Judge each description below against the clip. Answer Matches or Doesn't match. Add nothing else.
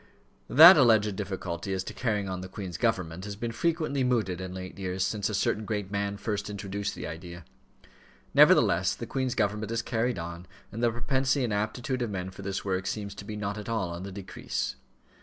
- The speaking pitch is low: Matches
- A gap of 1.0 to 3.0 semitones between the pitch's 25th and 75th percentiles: Doesn't match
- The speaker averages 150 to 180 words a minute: Doesn't match